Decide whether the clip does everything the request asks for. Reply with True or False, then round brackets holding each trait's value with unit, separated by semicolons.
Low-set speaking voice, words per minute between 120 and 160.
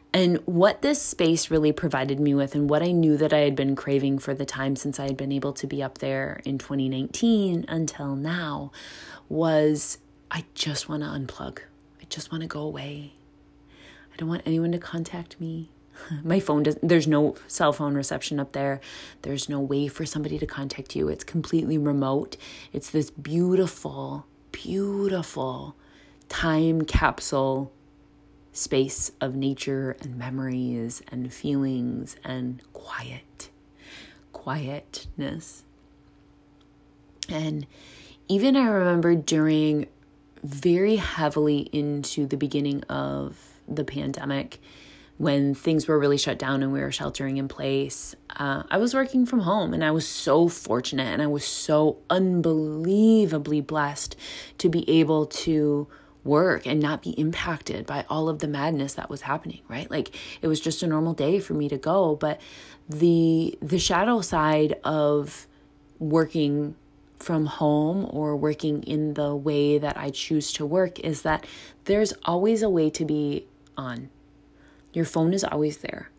False (150 Hz; 150 wpm)